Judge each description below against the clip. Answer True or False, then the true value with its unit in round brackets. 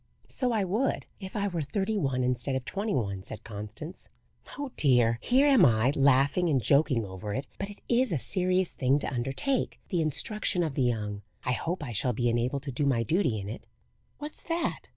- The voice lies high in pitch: False (140 Hz)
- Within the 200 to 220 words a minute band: True (205 wpm)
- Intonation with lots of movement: True (8.1 semitones)